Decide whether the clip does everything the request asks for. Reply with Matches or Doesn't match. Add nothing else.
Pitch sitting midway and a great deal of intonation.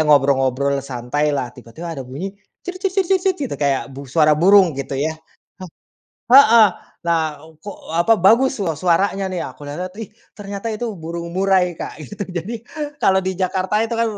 Matches